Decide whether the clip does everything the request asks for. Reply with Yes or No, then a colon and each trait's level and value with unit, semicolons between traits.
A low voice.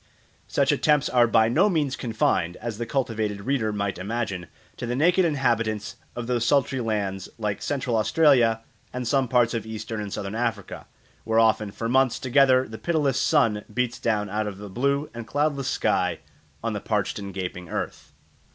Yes: low, 115 Hz